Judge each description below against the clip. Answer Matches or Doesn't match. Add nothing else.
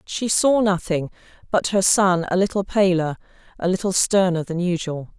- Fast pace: Doesn't match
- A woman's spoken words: Matches